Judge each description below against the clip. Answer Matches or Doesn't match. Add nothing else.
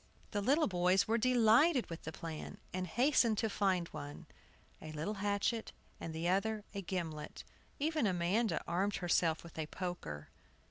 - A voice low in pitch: Doesn't match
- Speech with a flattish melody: Doesn't match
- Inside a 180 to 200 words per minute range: Doesn't match